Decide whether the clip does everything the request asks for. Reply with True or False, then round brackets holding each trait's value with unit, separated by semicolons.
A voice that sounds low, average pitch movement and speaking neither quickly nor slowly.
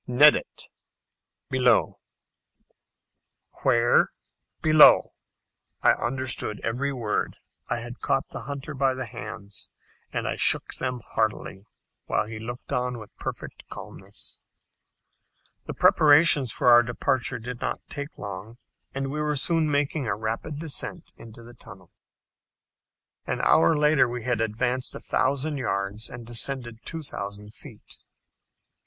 False (125 Hz; 3.7 semitones; 130 wpm)